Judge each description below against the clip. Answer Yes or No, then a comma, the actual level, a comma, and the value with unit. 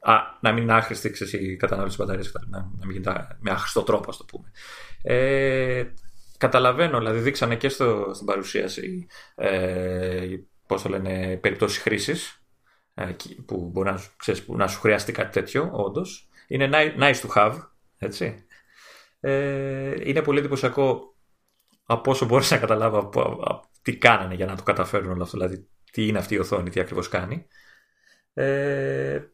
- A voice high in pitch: No, low, 105 Hz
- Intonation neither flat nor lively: No, wide, 5.9 semitones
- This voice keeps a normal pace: Yes, average, 160 wpm